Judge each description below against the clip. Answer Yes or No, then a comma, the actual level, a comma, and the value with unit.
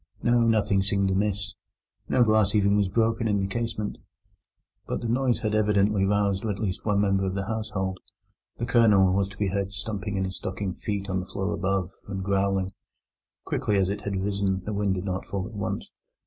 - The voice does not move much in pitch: Yes, narrow, 1.7 semitones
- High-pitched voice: No, low, 100 Hz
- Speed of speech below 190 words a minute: No, average, 200 wpm